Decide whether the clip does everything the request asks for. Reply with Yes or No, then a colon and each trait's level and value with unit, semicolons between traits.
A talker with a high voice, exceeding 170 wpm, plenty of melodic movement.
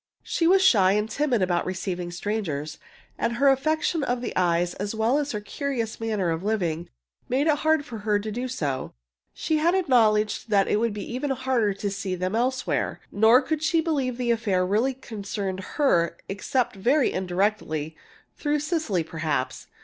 Yes: high, 220 Hz; average, 180 wpm; wide, 6.0 semitones